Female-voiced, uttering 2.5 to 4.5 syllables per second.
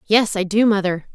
No: female; 5.2 syllables/s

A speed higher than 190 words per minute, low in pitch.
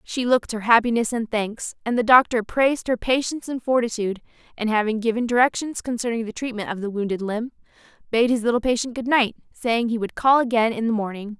No: fast, 205 wpm; high, 230 Hz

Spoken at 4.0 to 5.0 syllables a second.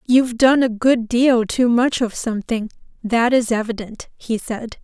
Yes: 4.5 syllables/s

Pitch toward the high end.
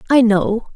Yes: high, 225 Hz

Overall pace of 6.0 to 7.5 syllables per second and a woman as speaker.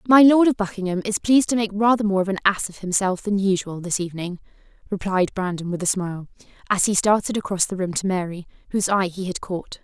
Yes: 6.2 syllables/s; female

